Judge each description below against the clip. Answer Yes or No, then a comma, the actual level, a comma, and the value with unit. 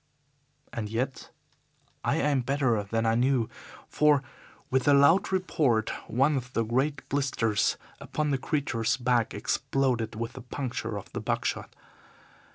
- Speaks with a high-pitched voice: No, low, 130 Hz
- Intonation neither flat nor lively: Yes, average, 3.7 semitones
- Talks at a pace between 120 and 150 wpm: Yes, average, 145 wpm